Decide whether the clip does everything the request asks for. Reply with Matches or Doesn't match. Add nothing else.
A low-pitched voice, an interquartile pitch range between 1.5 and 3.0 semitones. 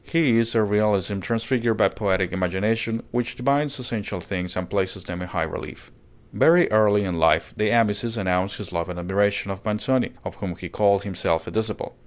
Doesn't match